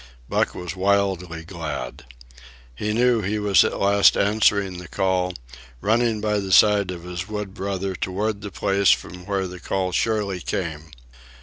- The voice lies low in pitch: Yes, very low, 95 Hz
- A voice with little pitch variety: Yes, narrow, 2.3 semitones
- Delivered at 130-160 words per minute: Yes, average, 155 wpm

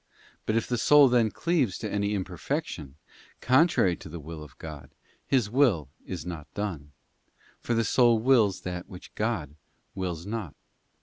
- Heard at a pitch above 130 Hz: No, low, 100 Hz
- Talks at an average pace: Yes, average, 165 wpm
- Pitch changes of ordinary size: No, wide, 6.3 semitones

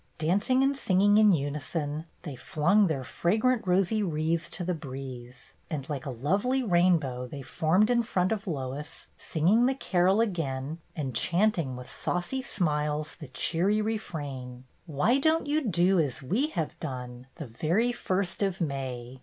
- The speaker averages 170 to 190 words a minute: No, average, 160 wpm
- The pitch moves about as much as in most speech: No, wide, 6.6 semitones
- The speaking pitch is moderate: Yes, medium, 170 Hz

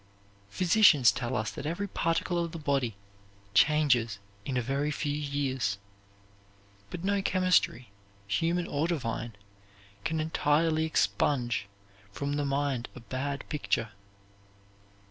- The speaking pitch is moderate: Yes, medium, 145 Hz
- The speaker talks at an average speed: No, slow, 120 wpm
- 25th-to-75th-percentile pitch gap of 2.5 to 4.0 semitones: No, average, 4.8 semitones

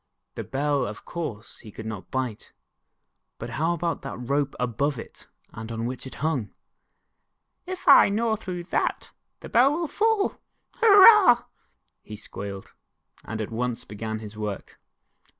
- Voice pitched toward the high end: No, low, 135 Hz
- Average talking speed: Yes, average, 150 wpm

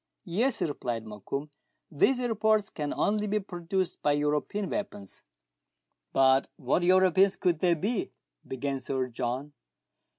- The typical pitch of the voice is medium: Yes, medium, 155 Hz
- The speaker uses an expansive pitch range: Yes, wide, 6.9 semitones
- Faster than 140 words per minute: No, slow, 135 wpm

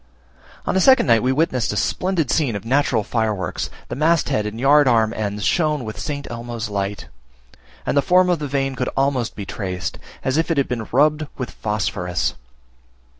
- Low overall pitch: Yes, low, 125 Hz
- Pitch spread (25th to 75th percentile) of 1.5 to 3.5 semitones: No, wide, 5.4 semitones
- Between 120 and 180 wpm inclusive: No, average, 190 wpm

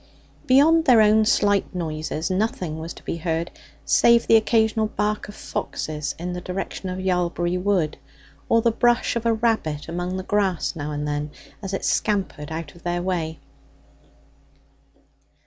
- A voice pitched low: No, medium, 185 Hz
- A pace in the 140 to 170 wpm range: Yes, average, 160 wpm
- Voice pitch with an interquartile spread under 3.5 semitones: No, average, 4.8 semitones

